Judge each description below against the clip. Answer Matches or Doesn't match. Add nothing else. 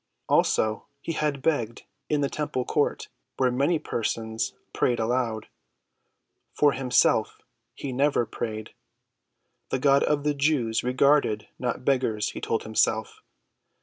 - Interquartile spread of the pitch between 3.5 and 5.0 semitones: Matches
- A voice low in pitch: Matches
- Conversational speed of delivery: Doesn't match